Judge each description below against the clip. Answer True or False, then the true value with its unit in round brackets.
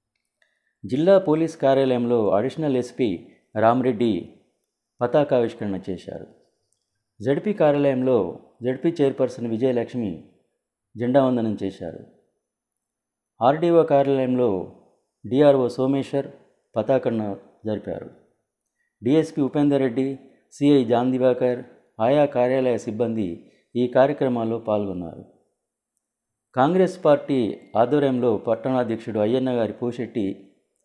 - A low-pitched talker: True (125 Hz)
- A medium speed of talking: True (80 wpm)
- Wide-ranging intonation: False (3.5 semitones)